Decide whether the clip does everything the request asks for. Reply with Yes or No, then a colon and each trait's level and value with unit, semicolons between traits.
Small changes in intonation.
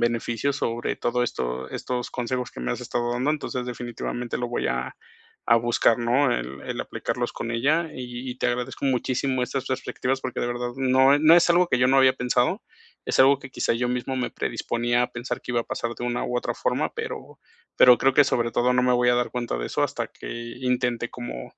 Yes: narrow, 1.6 semitones